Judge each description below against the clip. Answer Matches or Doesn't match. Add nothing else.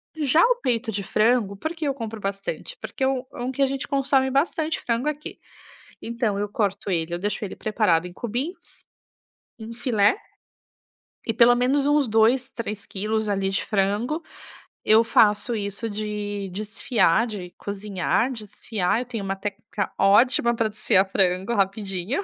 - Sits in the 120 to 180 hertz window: Doesn't match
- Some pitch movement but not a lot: Matches